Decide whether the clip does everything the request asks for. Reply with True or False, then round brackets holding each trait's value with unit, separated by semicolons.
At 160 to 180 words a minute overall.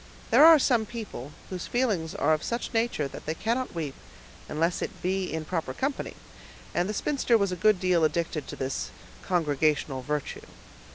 True (175 wpm)